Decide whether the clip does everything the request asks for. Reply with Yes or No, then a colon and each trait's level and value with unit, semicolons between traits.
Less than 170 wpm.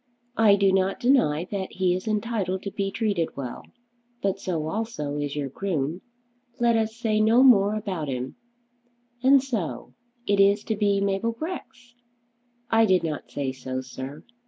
Yes: average, 160 wpm